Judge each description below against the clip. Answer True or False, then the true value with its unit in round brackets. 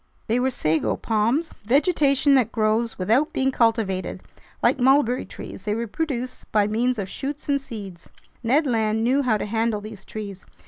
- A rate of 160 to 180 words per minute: True (165 wpm)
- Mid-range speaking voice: False (230 Hz)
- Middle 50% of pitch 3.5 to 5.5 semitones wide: True (3.9 semitones)